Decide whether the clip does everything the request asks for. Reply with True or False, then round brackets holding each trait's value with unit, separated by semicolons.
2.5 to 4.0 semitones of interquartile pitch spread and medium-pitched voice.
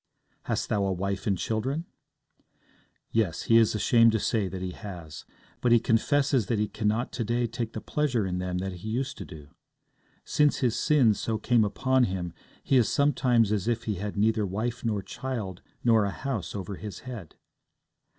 False (3.7 semitones; 110 Hz)